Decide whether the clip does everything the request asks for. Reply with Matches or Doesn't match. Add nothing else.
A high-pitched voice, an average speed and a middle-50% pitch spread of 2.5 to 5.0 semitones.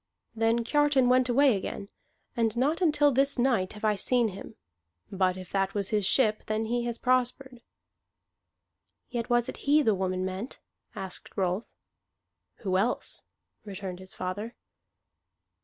Matches